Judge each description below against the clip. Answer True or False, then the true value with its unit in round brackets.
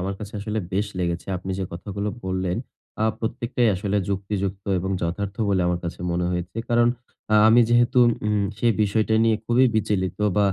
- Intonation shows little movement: False (3.0 semitones)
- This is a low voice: True (100 Hz)